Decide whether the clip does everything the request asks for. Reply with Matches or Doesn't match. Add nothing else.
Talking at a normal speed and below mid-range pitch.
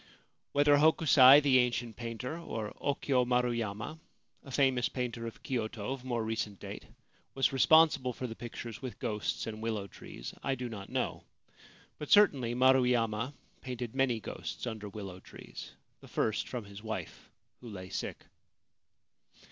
Matches